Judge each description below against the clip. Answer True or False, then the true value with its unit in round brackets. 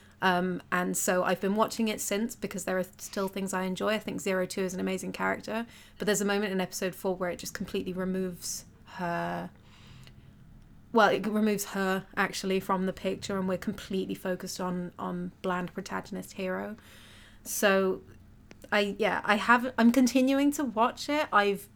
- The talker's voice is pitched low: False (190 Hz)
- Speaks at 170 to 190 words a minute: True (175 wpm)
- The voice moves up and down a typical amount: False (2.3 semitones)